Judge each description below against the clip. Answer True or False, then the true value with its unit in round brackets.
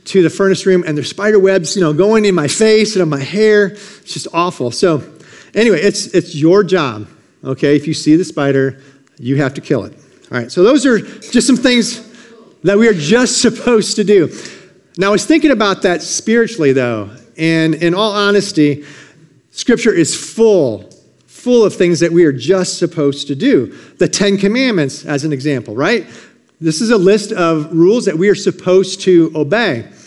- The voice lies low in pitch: False (185 Hz)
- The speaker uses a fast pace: False (195 wpm)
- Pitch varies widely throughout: True (5.8 semitones)